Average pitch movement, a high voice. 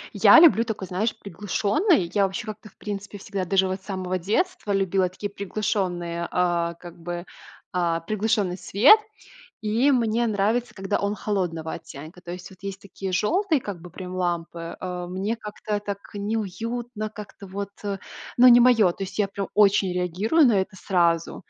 Yes: average, 3.1 semitones; high, 195 Hz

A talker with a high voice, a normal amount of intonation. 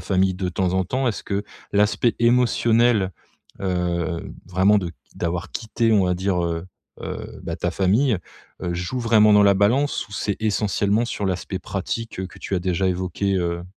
No: very low, 95 Hz; average, 3.1 semitones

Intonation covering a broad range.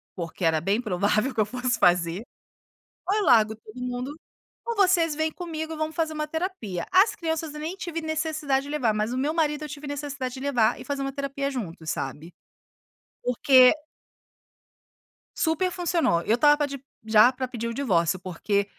Yes: wide, 6.5 semitones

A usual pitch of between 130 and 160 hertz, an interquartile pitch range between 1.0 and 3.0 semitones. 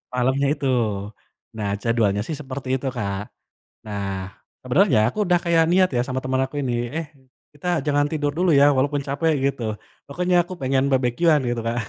No: medium, 140 Hz; average, 4.5 semitones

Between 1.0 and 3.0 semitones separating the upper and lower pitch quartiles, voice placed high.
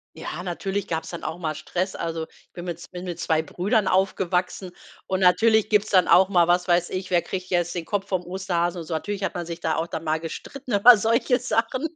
No: narrow, 2.6 semitones; medium, 180 Hz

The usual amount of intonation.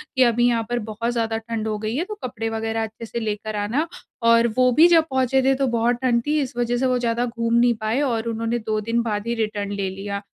No: narrow, 1.9 semitones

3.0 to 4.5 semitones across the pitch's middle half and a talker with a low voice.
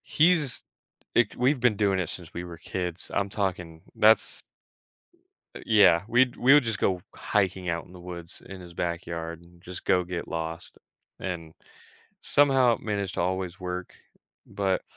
Yes: average, 3.8 semitones; very low, 90 Hz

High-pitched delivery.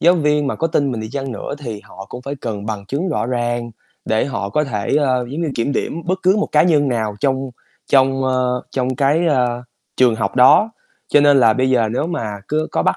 No: low, 130 Hz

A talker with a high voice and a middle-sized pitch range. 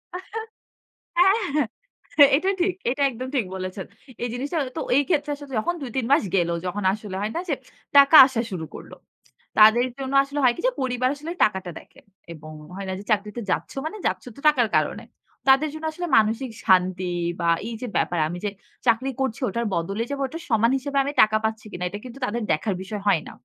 No: high, 235 Hz; wide, 5.8 semitones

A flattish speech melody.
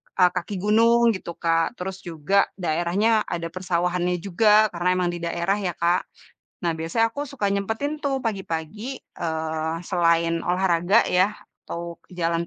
No: average, 3.7 semitones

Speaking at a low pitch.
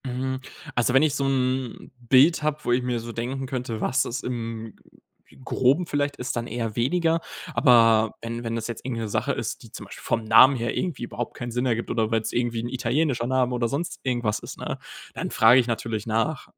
Yes: low, 120 Hz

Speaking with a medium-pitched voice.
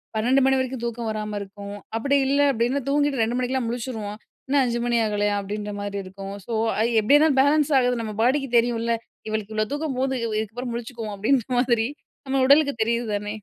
No: high, 235 Hz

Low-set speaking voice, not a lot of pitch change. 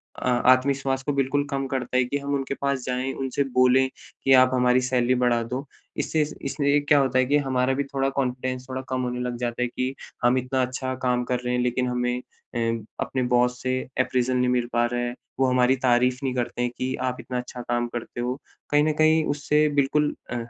Yes: low, 130 Hz; narrow, 1.6 semitones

